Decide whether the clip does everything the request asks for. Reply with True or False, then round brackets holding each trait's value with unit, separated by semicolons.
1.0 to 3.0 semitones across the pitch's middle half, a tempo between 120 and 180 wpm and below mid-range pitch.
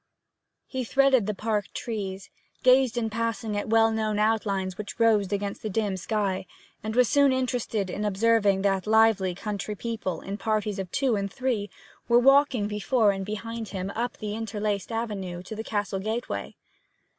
False (2.4 semitones; 170 wpm; 215 Hz)